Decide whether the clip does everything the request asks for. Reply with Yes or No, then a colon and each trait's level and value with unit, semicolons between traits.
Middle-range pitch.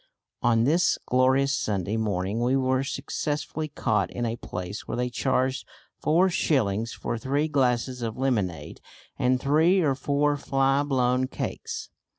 No: low, 130 Hz